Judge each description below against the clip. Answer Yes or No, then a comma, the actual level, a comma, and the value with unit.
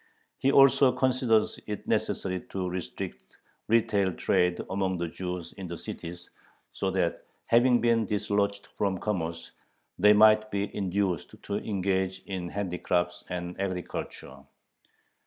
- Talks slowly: Yes, slow, 125 wpm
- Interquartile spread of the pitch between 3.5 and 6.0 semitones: No, average, 3.0 semitones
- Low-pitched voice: Yes, very low, 95 Hz